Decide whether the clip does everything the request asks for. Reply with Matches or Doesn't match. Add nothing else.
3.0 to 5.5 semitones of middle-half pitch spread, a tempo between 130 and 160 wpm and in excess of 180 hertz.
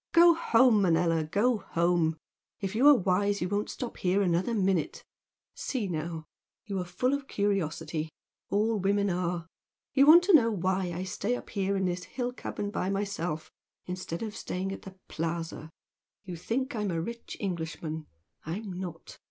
Doesn't match